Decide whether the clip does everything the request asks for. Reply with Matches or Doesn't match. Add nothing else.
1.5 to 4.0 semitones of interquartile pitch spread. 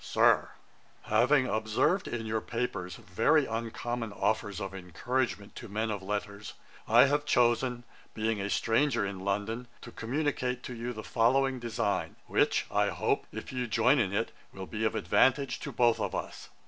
Matches